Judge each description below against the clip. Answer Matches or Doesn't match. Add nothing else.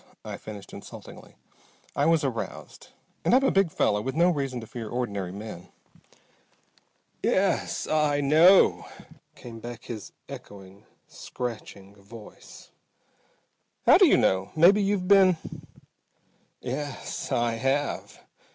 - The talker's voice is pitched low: Matches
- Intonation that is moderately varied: Doesn't match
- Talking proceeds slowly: Matches